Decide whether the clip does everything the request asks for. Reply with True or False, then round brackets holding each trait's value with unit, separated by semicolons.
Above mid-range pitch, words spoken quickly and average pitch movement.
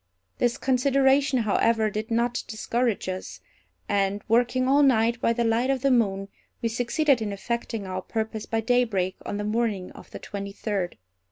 False (230 Hz; 170 wpm; 3.1 semitones)